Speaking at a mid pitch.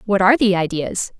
No: high, 200 Hz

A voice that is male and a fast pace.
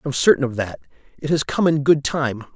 Yes: male; fast, 235 wpm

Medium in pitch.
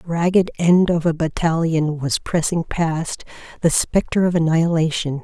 Yes: medium, 165 Hz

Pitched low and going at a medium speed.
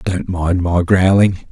Yes: very low, 90 Hz; average, 160 wpm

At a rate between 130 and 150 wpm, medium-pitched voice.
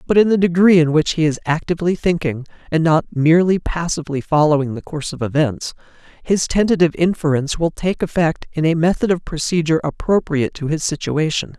No: average, 175 wpm; medium, 160 Hz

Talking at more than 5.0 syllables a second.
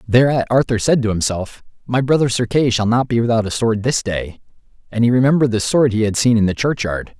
Yes: 5.9 syllables/s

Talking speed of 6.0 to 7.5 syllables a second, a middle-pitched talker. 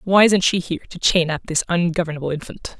Yes: 6.3 syllables/s; medium, 170 Hz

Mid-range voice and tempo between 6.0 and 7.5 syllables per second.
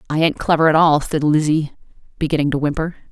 Yes: medium, 155 Hz; 6.4 syllables/s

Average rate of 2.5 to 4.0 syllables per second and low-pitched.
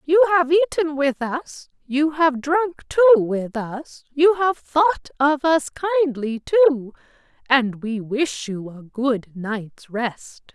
No: 3.6 syllables/s; very high, 275 Hz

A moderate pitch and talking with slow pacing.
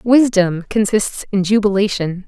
No: high, 200 Hz; slow, 105 wpm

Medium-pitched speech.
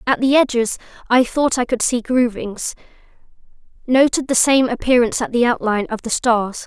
No: high, 245 Hz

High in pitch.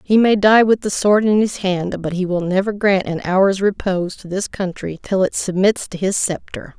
Yes: high, 195 Hz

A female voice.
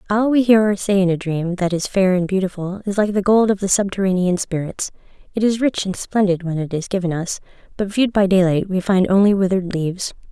Yes: female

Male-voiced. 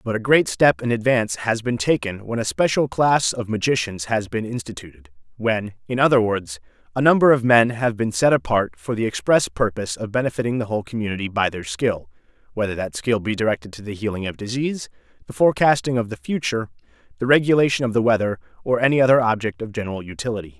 Yes: male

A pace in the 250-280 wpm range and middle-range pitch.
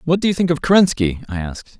Yes: fast, 270 wpm; medium, 145 Hz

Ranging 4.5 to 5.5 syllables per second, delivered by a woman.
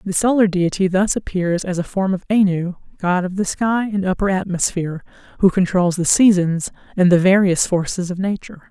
Yes: 5.4 syllables/s; female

